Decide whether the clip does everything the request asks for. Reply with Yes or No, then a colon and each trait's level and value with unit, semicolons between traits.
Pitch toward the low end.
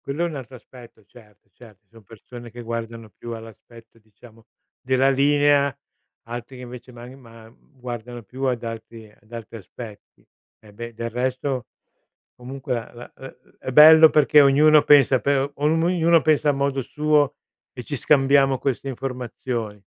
Yes: low, 125 Hz